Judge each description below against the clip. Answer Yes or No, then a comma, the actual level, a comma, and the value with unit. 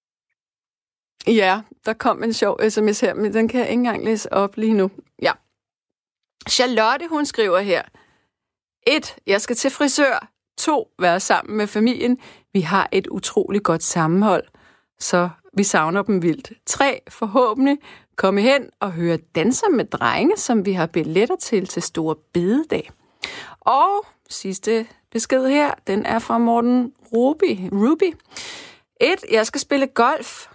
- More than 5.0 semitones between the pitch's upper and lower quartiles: Yes, wide, 5.6 semitones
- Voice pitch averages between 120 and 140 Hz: No, high, 225 Hz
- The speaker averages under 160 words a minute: Yes, slow, 145 wpm